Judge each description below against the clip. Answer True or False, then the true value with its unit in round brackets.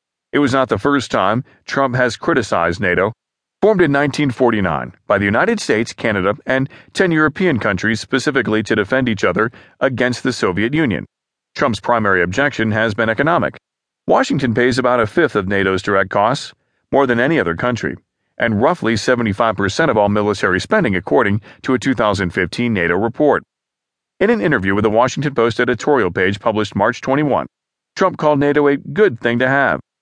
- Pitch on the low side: True (120 Hz)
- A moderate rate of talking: True (170 wpm)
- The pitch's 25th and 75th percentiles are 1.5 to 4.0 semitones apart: False (4.4 semitones)